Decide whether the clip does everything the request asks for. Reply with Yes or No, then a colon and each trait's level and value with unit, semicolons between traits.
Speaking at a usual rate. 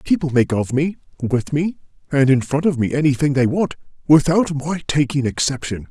Yes: average, 185 wpm